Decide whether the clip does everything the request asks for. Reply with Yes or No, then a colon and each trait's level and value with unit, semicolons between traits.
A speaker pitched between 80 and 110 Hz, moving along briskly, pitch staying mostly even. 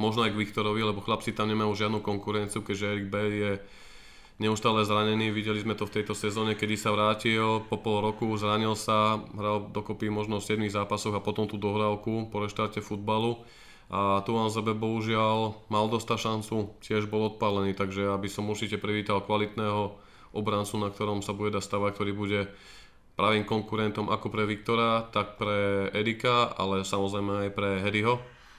Yes: low, 105 Hz; fast, 170 wpm; narrow, 1.0 semitones